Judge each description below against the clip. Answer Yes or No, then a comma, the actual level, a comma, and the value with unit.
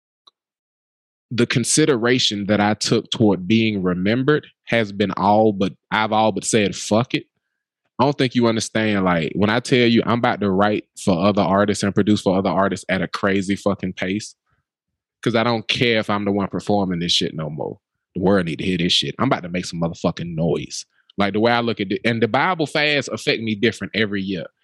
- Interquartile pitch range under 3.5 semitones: Yes, average, 3.0 semitones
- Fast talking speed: Yes, fast, 215 wpm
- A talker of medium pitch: No, low, 105 Hz